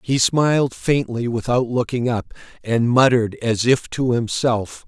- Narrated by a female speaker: No, male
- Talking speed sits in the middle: Yes, average, 150 wpm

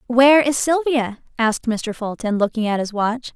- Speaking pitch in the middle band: No, high, 240 Hz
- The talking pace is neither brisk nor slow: Yes, average, 180 wpm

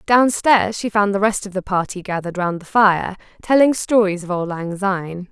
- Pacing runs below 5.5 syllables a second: Yes, 5.3 syllables/s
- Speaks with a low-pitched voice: No, high, 195 Hz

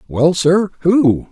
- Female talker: No, male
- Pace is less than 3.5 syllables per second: Yes, 3.0 syllables/s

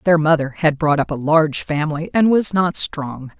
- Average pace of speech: No, fast, 210 wpm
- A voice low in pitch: No, medium, 155 Hz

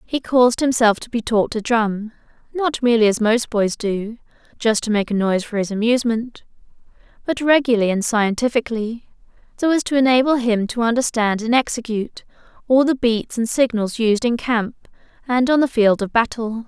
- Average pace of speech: Yes, average, 175 wpm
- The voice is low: No, high, 230 Hz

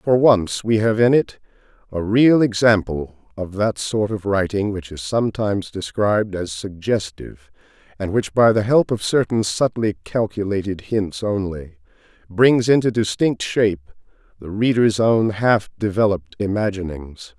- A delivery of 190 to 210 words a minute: No, average, 140 wpm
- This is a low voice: Yes, low, 105 Hz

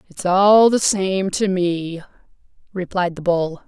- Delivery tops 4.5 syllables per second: No, 3.6 syllables/s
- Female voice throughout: Yes, female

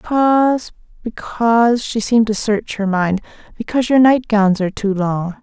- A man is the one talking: No, female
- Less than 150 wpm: Yes, slow, 135 wpm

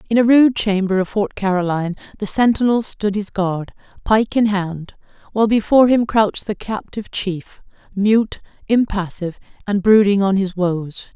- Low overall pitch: No, high, 205 Hz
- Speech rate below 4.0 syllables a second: No, 4.9 syllables/s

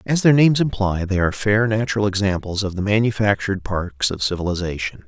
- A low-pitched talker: Yes, low, 100 Hz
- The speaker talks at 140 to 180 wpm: Yes, average, 175 wpm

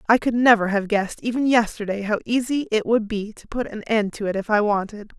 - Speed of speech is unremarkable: No, fast, 245 wpm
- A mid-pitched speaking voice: No, high, 220 Hz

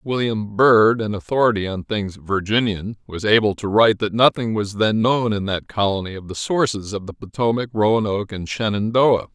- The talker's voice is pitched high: No, low, 105 Hz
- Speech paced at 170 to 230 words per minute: Yes, average, 180 wpm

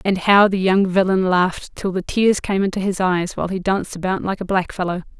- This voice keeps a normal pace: No, fast, 230 wpm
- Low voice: No, high, 190 Hz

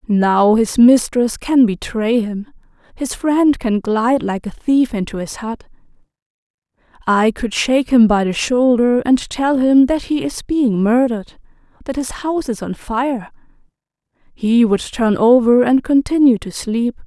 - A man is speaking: No, female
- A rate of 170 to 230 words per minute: No, average, 160 wpm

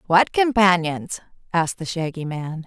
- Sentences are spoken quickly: No, slow, 135 wpm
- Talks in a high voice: No, medium, 175 Hz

